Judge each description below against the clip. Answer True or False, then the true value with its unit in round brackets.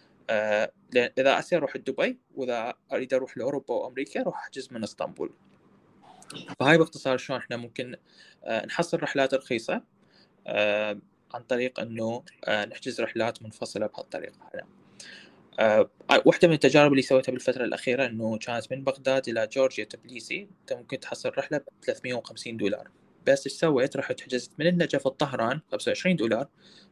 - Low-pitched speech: True (130 Hz)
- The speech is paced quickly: True (140 wpm)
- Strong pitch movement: False (3.5 semitones)